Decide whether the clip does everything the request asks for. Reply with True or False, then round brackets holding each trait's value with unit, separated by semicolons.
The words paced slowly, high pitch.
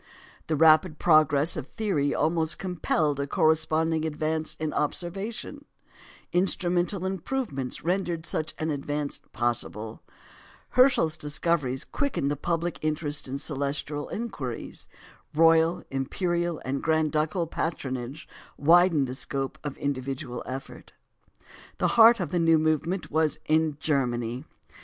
False (115 wpm; 155 Hz)